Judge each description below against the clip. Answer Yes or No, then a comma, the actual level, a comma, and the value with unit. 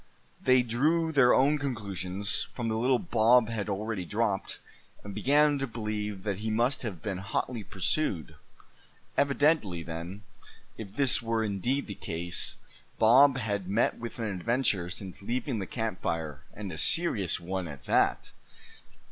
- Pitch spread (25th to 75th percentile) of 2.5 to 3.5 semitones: No, average, 4.7 semitones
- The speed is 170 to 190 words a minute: No, average, 150 wpm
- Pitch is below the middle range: Yes, low, 110 Hz